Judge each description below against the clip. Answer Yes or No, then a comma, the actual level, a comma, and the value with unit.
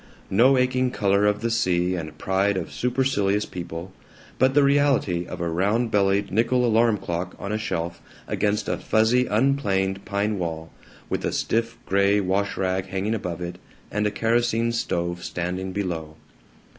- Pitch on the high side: No, low, 100 Hz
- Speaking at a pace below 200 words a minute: Yes, average, 160 wpm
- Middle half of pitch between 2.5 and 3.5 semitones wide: No, average, 4.0 semitones